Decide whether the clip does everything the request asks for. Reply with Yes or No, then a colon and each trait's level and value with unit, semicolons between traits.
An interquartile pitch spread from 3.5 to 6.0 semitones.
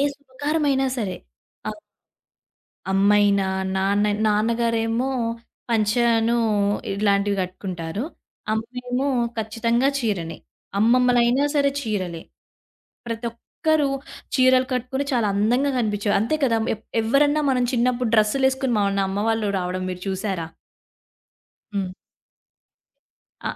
Yes: average, 3.9 semitones